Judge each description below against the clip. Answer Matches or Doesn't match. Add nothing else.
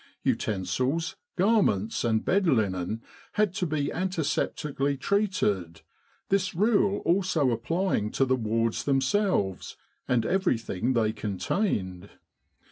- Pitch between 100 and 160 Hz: Matches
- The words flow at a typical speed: Doesn't match